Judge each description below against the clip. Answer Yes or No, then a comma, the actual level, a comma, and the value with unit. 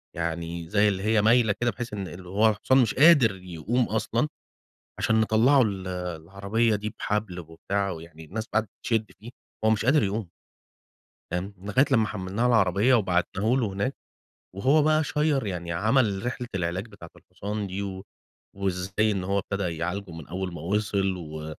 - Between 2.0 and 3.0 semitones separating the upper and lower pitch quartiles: No, average, 3.6 semitones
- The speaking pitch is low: Yes, low, 100 Hz